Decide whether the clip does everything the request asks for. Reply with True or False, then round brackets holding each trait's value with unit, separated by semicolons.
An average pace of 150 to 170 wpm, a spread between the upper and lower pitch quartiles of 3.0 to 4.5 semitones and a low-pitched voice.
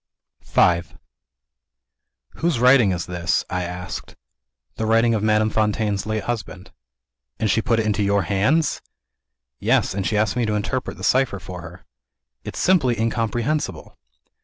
False (140 wpm; 3.5 semitones; 110 Hz)